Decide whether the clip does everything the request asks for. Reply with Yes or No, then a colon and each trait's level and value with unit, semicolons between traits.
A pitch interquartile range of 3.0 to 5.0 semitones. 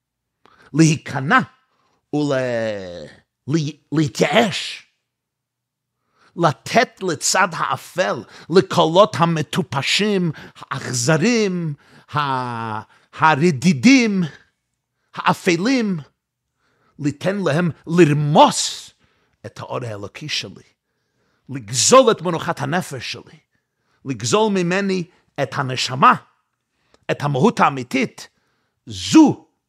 No: wide, 5.5 semitones